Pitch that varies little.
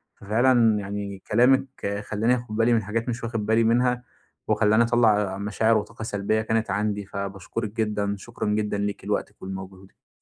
Yes: narrow, 2.2 semitones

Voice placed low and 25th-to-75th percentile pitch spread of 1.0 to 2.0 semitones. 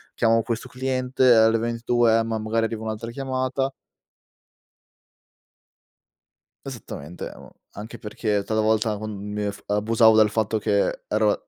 Yes: low, 110 Hz; narrow, 1.7 semitones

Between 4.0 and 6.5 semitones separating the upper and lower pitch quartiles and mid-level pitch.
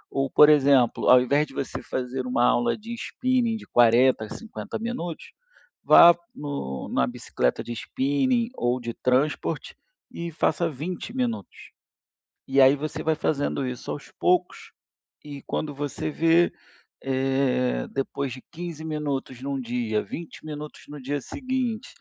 Yes: average, 4.8 semitones; medium, 145 Hz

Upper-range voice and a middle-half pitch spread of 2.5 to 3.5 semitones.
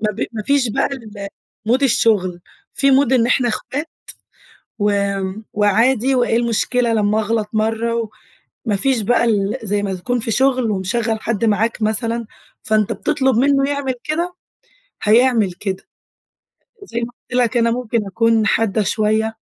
Yes: high, 225 Hz; average, 2.9 semitones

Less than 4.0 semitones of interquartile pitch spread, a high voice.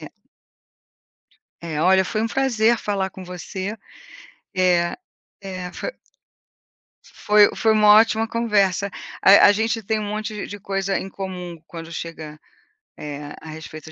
Yes: average, 3.3 semitones; high, 195 Hz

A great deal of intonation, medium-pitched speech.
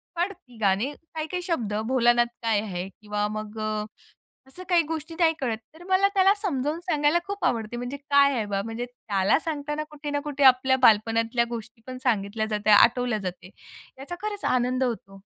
No: wide, 5.7 semitones; very high, 250 Hz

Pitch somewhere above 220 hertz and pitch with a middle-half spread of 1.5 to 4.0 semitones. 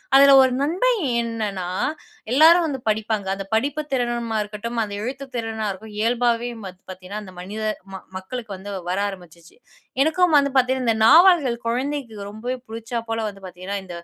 No: high, 230 Hz; average, 4.5 semitones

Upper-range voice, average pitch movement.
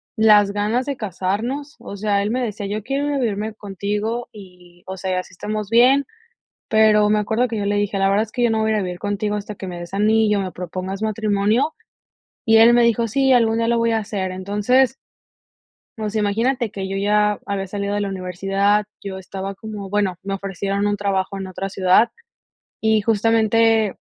No: high, 210 Hz; narrow, 2.2 semitones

